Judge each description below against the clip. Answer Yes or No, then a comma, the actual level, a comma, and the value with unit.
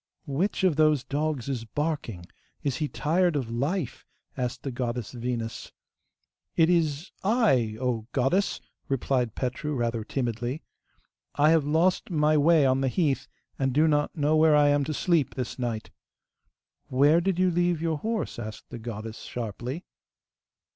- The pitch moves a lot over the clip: No, average, 4.7 semitones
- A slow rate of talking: No, average, 155 wpm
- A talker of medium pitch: Yes, medium, 145 Hz